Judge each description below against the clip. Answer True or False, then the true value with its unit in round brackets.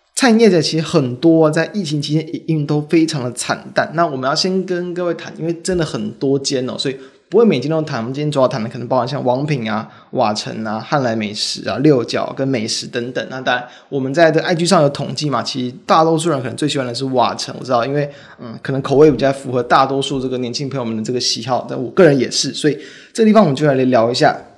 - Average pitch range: True (4.0 semitones)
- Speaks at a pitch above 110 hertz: True (140 Hz)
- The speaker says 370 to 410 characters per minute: True (380 characters per minute)